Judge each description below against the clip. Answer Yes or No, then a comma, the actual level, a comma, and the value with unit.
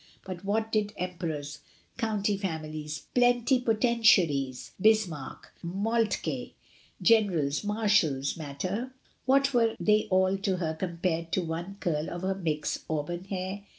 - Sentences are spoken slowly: Yes, slow, 125 wpm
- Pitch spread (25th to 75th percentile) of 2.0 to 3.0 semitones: No, average, 5.0 semitones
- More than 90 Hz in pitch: Yes, medium, 185 Hz